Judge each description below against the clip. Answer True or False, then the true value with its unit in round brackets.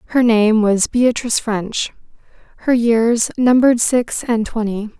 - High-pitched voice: True (230 Hz)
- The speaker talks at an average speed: False (130 wpm)